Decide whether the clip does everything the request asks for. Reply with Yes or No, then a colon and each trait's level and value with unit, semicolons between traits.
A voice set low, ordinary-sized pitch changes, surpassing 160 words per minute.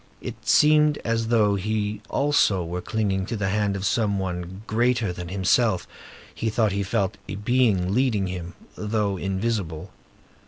No: low, 105 Hz; average, 3.2 semitones; average, 155 wpm